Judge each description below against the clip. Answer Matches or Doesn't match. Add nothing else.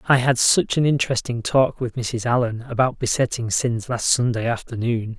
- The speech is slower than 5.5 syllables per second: Matches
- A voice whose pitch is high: Doesn't match